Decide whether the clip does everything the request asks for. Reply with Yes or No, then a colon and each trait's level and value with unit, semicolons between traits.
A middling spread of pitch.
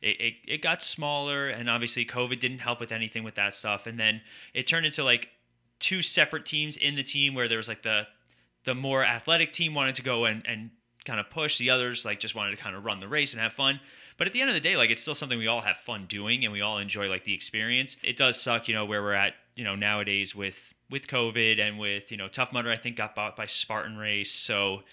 Yes: average, 3.9 semitones